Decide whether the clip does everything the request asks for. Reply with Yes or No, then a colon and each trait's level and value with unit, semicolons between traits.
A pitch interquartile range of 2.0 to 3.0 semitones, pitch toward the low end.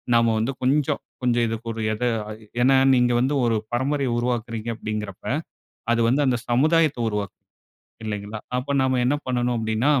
Yes: narrow, 2.6 semitones; low, 120 Hz